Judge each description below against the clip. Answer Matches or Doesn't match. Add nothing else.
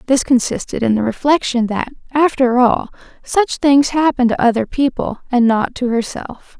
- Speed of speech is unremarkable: Matches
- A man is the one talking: Doesn't match